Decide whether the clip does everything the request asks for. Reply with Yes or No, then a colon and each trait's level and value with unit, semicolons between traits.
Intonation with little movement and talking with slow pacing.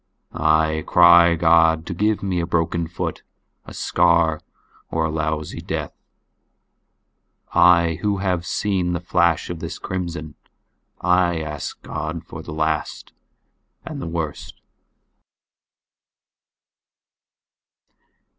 Yes: narrow, 1.8 semitones; slow, 100 wpm